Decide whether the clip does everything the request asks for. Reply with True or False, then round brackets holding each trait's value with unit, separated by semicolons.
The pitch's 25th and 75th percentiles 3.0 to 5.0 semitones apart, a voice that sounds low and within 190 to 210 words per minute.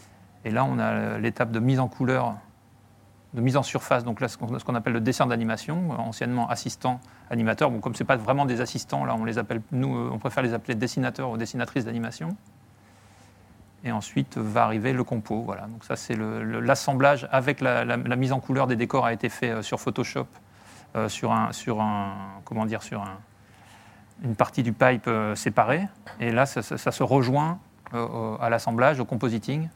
False (2.6 semitones; 120 Hz; 200 wpm)